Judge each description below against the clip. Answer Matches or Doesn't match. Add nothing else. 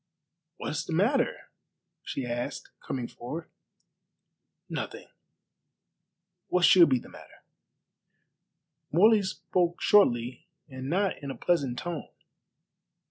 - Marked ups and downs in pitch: Matches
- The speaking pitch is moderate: Matches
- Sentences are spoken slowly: Matches